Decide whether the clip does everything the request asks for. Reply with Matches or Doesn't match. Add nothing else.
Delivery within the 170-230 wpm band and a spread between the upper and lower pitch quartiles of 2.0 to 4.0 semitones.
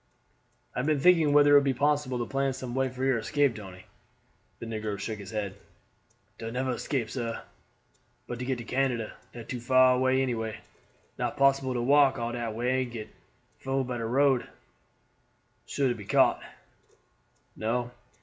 Matches